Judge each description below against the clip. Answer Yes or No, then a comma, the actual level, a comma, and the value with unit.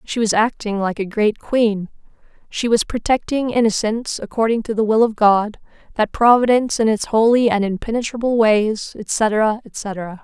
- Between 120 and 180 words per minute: Yes, average, 160 wpm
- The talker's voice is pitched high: Yes, high, 220 Hz